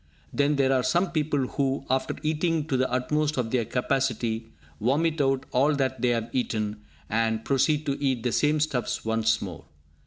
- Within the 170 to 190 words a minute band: Yes, average, 180 wpm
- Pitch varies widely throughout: No, average, 4.0 semitones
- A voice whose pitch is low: Yes, low, 130 Hz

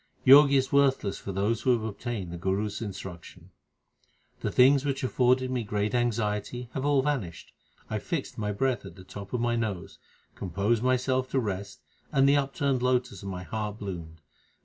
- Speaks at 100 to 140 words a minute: No, average, 180 wpm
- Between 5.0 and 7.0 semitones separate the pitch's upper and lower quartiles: No, average, 4.5 semitones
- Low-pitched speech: Yes, low, 115 Hz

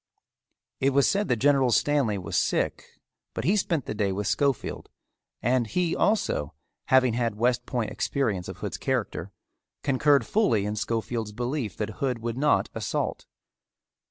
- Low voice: Yes, low, 125 Hz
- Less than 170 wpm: Yes, average, 155 wpm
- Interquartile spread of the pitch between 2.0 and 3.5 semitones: No, average, 4.6 semitones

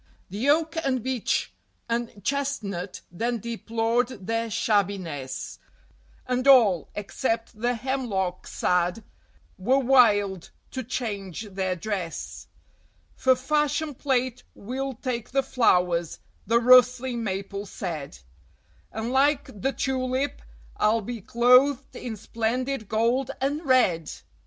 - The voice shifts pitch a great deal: No, average, 4.5 semitones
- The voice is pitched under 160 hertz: No, high, 235 Hz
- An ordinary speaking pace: No, slow, 110 wpm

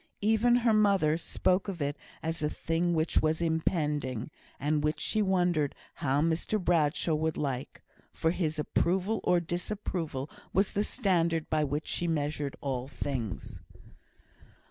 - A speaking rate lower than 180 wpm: Yes, average, 145 wpm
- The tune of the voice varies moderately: Yes, average, 3.5 semitones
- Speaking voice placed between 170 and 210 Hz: No, medium, 160 Hz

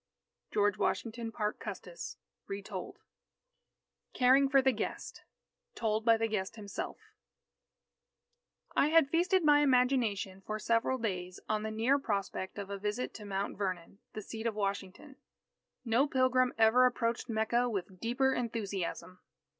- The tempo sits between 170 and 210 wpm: No, slow, 135 wpm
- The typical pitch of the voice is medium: No, high, 225 Hz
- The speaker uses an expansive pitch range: No, average, 3.9 semitones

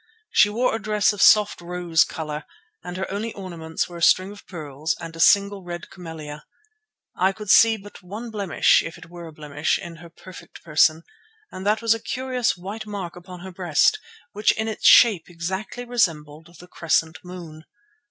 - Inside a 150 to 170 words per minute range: No, average, 185 wpm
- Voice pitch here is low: No, medium, 180 Hz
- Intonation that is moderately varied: Yes, average, 4.0 semitones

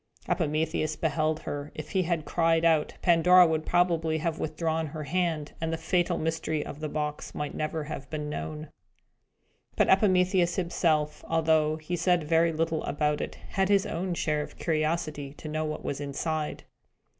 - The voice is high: No, medium, 160 Hz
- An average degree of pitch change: No, narrow, 1.9 semitones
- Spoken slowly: No, average, 165 wpm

